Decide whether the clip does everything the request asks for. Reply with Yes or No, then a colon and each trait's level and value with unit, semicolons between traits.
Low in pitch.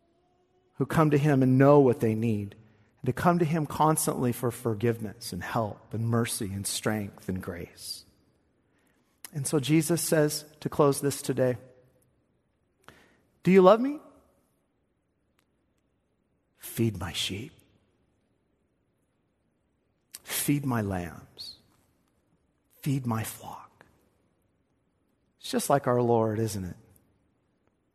Yes: low, 120 Hz